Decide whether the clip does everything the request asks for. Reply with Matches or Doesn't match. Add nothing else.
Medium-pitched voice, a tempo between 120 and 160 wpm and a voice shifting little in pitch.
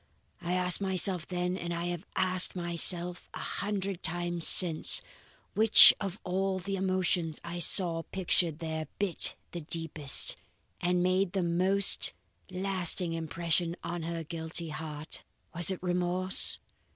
Matches